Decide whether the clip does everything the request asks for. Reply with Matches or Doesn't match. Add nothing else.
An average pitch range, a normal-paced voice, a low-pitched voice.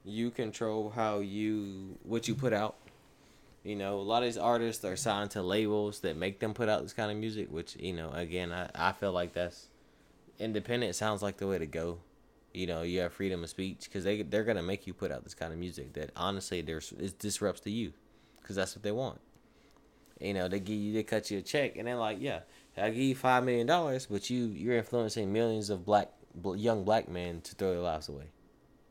Doesn't match